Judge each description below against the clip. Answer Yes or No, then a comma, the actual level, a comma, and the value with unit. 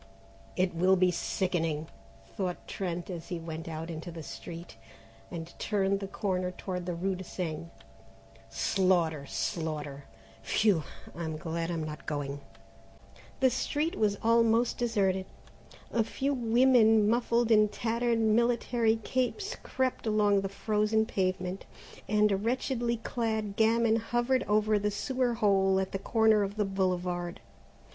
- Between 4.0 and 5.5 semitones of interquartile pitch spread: Yes, average, 4.5 semitones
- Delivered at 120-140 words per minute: Yes, slow, 135 wpm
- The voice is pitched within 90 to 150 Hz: No, high, 200 Hz